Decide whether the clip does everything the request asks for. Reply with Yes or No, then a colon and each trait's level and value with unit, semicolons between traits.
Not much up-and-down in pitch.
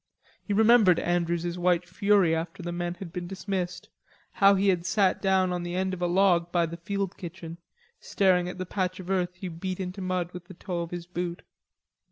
Yes: narrow, 1.5 semitones